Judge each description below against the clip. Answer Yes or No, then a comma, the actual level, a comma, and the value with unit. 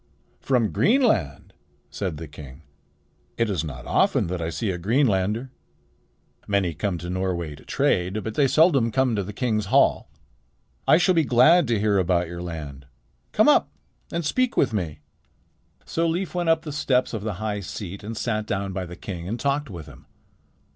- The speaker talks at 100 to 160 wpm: No, average, 180 wpm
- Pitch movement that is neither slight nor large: No, wide, 6.8 semitones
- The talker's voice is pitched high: No, low, 105 Hz